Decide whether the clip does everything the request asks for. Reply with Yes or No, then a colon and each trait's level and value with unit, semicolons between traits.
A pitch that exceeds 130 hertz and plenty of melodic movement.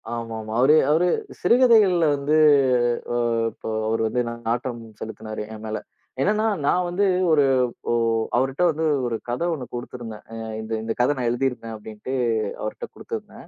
No: low, 125 Hz; wide, 6.0 semitones